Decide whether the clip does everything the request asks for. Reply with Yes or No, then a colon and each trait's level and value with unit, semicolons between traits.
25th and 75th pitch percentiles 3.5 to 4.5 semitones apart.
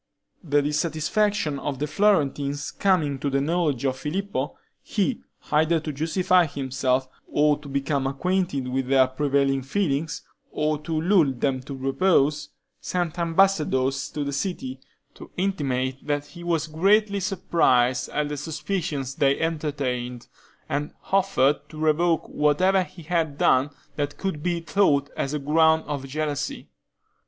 Yes: average, 3.8 semitones